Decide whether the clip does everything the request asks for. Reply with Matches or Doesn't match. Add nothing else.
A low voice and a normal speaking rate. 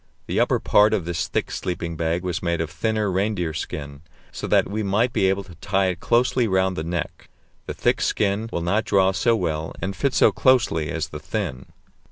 Doesn't match